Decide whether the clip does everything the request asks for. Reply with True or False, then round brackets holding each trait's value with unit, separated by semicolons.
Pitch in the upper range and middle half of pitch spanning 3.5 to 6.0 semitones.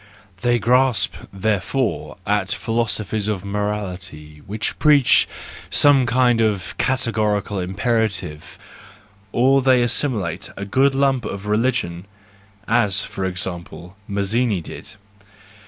False (105 Hz; 4.3 semitones)